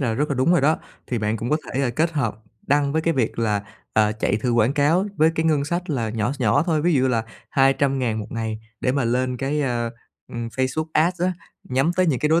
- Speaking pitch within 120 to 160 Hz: Yes, low, 135 Hz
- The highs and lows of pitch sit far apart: No, average, 4.9 semitones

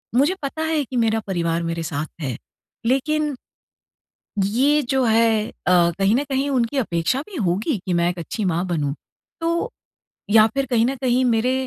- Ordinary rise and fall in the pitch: No, wide, 7.4 semitones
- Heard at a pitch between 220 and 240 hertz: Yes, high, 230 Hz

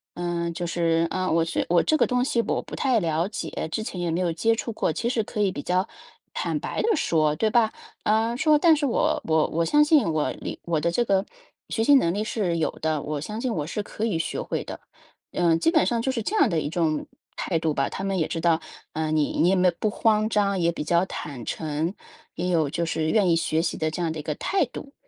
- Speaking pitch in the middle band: Yes, medium, 175 Hz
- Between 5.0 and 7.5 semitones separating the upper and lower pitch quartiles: Yes, wide, 5.5 semitones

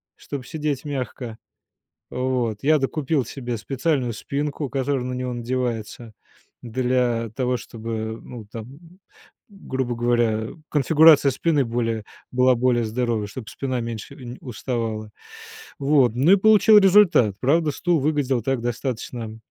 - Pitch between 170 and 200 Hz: No, low, 125 Hz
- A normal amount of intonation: Yes, average, 3.4 semitones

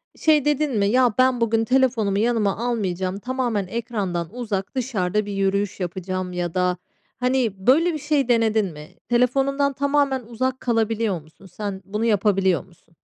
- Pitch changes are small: No, average, 5.0 semitones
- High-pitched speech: Yes, high, 220 Hz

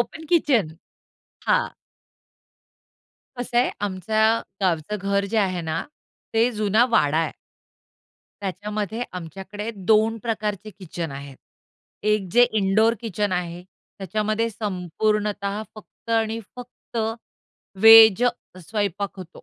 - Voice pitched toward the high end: Yes, high, 210 Hz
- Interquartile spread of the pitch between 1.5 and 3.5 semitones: Yes, average, 3.1 semitones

